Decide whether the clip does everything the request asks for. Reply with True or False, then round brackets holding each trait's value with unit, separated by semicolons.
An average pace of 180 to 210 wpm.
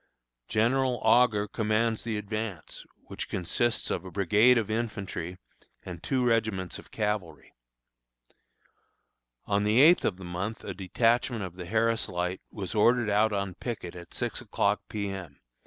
False (150 wpm)